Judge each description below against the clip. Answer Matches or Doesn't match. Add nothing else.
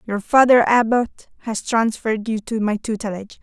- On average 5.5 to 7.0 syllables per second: Doesn't match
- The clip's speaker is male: Doesn't match